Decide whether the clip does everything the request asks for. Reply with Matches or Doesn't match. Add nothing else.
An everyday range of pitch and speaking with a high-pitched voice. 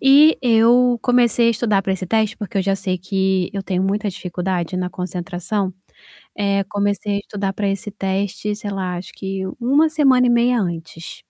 Matches